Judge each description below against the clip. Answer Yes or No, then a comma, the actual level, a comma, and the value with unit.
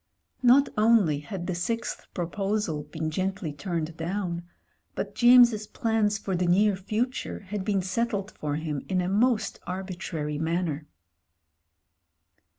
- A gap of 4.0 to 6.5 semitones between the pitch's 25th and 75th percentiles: Yes, average, 4.3 semitones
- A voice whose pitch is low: No, high, 190 Hz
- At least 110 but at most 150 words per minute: Yes, slow, 135 wpm